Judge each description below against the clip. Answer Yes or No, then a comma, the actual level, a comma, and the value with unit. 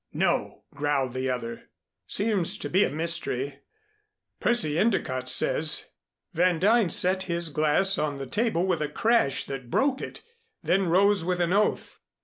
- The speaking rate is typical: Yes, average, 155 wpm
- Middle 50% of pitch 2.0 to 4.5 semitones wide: No, wide, 5.4 semitones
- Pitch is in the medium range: Yes, medium, 170 Hz